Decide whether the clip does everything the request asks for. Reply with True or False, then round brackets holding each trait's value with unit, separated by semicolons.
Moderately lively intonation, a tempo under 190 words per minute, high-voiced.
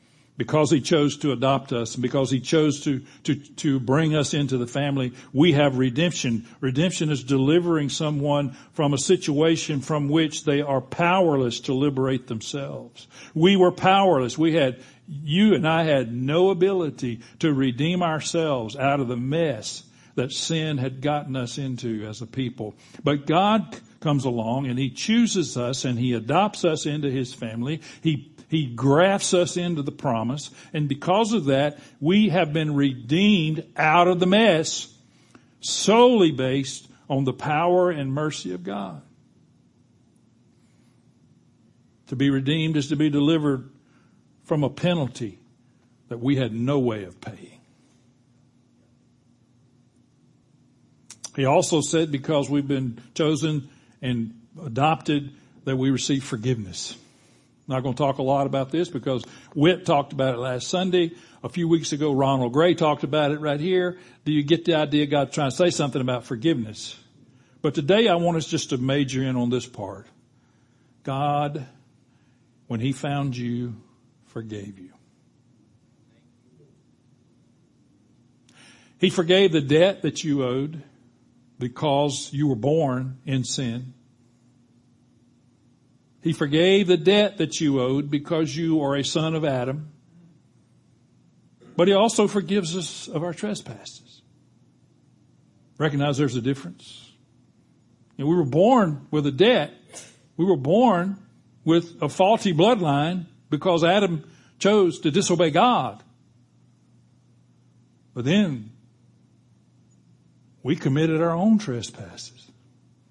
False (4.5 semitones; 140 wpm; 140 Hz)